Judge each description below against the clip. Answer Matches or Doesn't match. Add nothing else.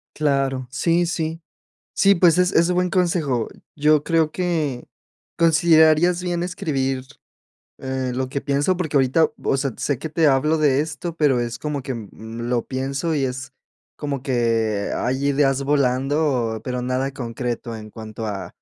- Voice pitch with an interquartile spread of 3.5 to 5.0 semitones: Matches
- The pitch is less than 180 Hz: Matches